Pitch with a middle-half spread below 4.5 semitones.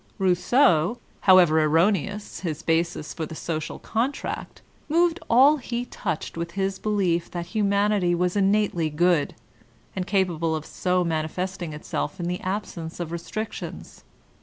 Yes: average, 3.7 semitones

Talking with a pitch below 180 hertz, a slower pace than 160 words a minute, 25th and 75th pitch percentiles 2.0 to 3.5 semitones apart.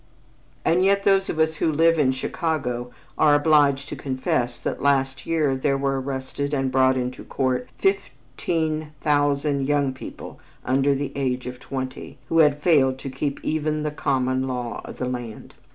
No: medium, 140 Hz; average, 170 wpm; average, 2.7 semitones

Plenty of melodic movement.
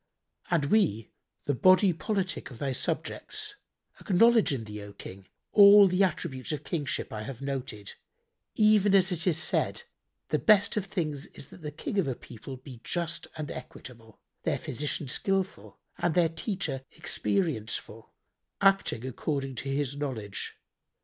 Yes: wide, 6.7 semitones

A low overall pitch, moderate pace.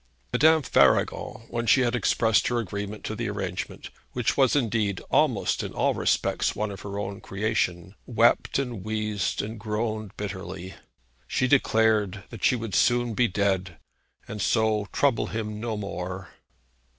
Yes: low, 110 Hz; average, 150 wpm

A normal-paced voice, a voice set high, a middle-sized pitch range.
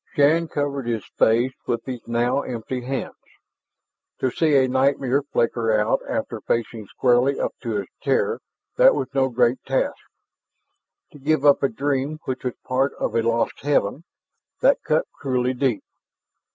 No: average, 155 wpm; low, 130 Hz; average, 3.0 semitones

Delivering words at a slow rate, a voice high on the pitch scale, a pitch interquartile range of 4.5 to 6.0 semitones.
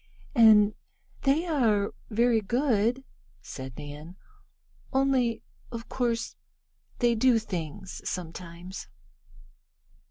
Yes: slow, 85 wpm; high, 225 Hz; average, 5.1 semitones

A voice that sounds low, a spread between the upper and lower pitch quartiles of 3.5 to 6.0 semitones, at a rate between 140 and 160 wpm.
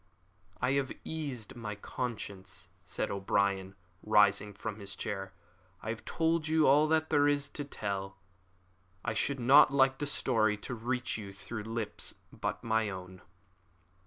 Yes: low, 110 Hz; wide, 5.5 semitones; average, 155 wpm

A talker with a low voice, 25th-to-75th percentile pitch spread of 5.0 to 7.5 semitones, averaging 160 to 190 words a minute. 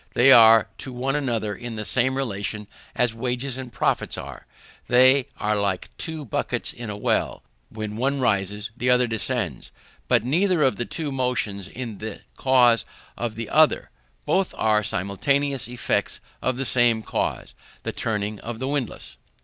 No: low, 120 Hz; average, 3.5 semitones; average, 165 wpm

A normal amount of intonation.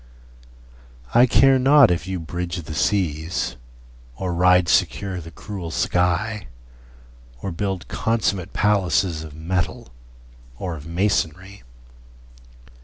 Yes: average, 3.3 semitones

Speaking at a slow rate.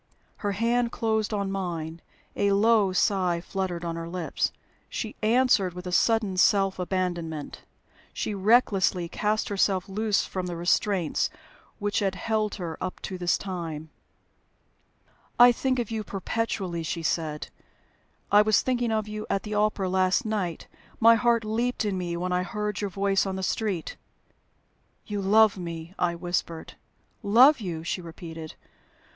No: average, 150 wpm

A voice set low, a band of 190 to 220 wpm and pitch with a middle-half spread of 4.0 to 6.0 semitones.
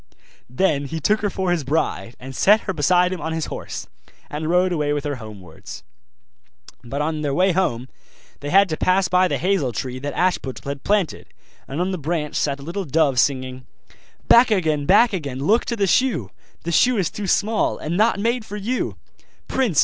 No: medium, 165 Hz; average, 200 wpm; wide, 5.6 semitones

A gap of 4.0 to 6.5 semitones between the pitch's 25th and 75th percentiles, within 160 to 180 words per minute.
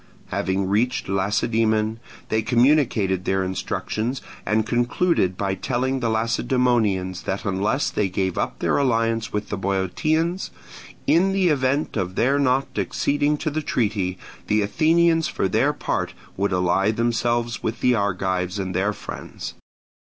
No: average, 5.0 semitones; average, 140 wpm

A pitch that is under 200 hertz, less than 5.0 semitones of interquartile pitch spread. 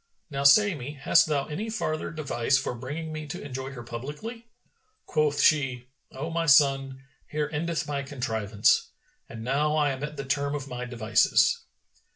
Yes: medium, 140 Hz; average, 2.8 semitones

